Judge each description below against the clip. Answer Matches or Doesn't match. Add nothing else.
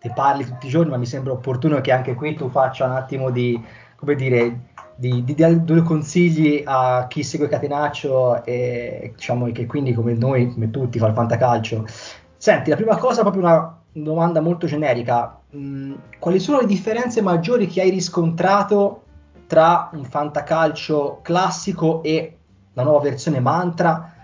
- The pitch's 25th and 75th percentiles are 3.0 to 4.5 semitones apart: Doesn't match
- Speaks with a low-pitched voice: Doesn't match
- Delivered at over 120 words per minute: Matches